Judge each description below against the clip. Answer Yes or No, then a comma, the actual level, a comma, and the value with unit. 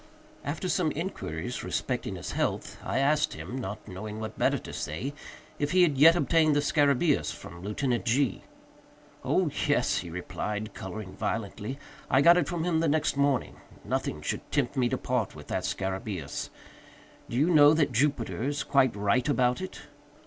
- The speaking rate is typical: Yes, average, 170 wpm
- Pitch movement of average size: No, wide, 6.1 semitones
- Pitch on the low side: Yes, low, 130 Hz